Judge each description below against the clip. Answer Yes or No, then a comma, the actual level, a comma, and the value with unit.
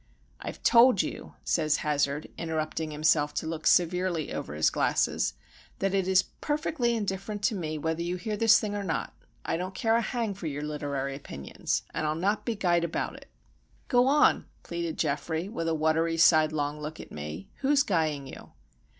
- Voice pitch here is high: No, medium, 165 Hz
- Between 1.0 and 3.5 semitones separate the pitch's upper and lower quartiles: No, average, 4.9 semitones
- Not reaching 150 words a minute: No, average, 175 wpm